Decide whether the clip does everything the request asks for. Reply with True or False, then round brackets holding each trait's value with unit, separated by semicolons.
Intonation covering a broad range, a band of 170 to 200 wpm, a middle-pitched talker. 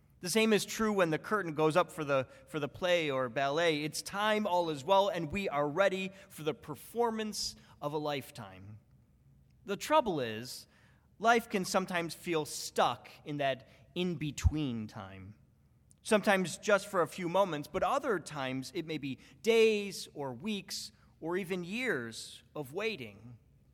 False (6.1 semitones; 160 wpm; 165 Hz)